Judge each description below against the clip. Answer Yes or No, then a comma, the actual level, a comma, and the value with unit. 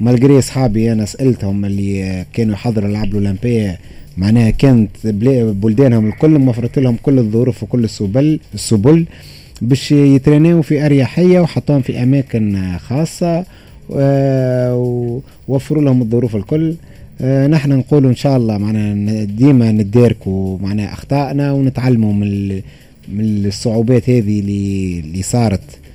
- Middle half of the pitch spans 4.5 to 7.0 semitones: Yes, average, 4.8 semitones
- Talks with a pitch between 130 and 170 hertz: No, low, 120 Hz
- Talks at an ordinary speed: Yes, average, 110 wpm